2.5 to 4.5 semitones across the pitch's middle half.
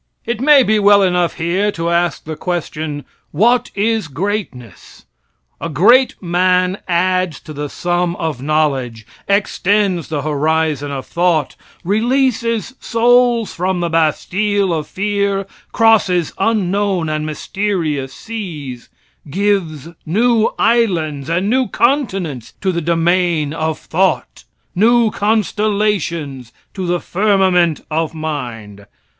No: average, 4.9 semitones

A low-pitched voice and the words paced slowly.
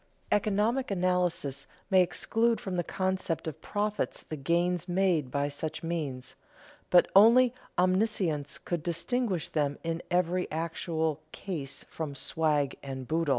No: medium, 170 Hz; slow, 130 wpm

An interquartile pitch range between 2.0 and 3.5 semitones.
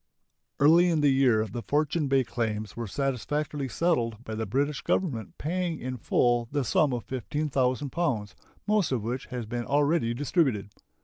No: average, 4.3 semitones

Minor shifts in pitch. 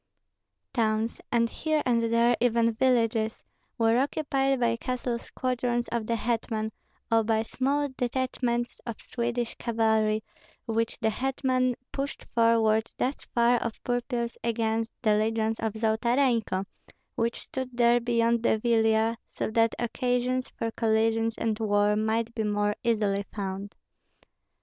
Yes: narrow, 1.7 semitones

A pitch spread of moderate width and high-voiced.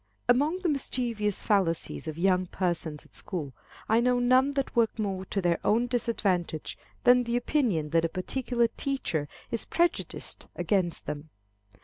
No: wide, 6.2 semitones; high, 210 Hz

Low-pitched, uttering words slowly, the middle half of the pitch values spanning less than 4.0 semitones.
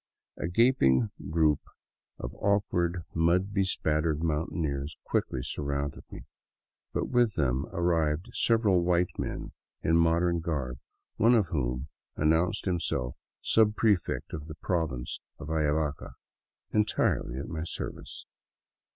Yes: very low, 80 Hz; slow, 120 wpm; average, 3.6 semitones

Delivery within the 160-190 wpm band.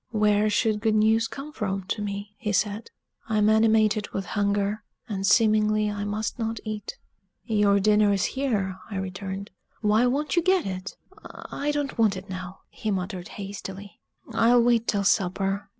Yes: average, 165 wpm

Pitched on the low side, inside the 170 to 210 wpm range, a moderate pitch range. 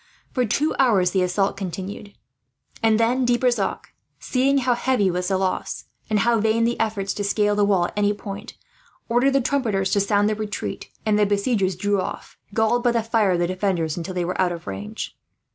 No: high, 205 Hz; fast, 205 wpm; average, 3.4 semitones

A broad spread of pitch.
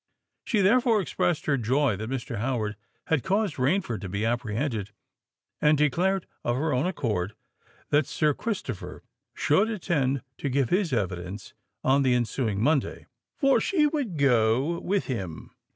Yes: wide, 7.4 semitones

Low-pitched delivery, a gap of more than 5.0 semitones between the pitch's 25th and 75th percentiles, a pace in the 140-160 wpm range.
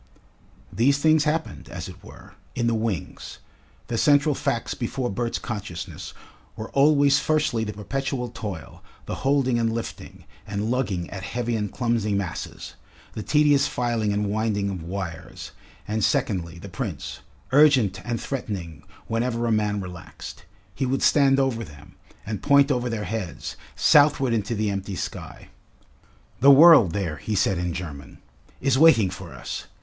Yes: low, 115 Hz; wide, 5.4 semitones; average, 155 wpm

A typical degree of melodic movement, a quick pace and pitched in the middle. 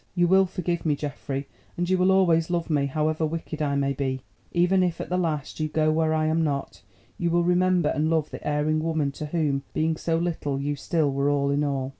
Yes: average, 3.0 semitones; fast, 230 wpm; medium, 155 Hz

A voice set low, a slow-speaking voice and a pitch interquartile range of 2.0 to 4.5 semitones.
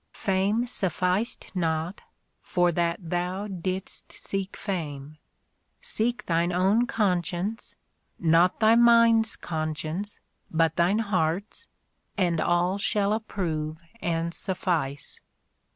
No: medium, 180 Hz; slow, 105 wpm; average, 3.6 semitones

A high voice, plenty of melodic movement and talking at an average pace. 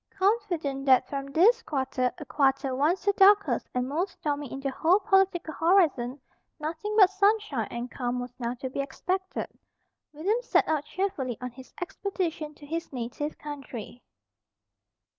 Yes: very high, 300 Hz; wide, 6.2 semitones; average, 155 wpm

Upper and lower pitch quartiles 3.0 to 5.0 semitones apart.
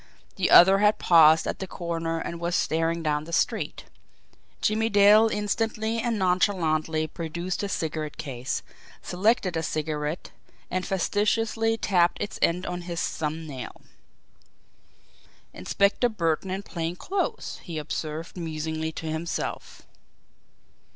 Yes: average, 4.2 semitones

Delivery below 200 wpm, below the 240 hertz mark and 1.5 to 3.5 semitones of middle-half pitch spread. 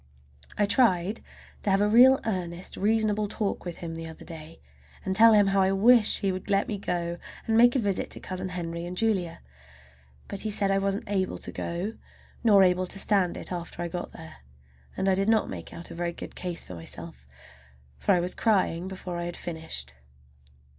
No: fast, 205 wpm; high, 190 Hz; average, 3.2 semitones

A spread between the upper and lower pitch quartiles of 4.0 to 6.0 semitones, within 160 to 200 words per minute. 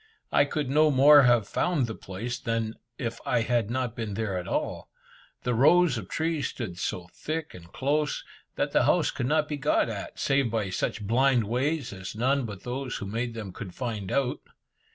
Yes: average, 4.4 semitones; average, 195 wpm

